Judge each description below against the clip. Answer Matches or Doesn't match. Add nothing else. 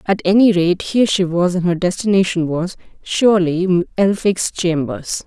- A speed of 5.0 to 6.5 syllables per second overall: Doesn't match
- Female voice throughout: Matches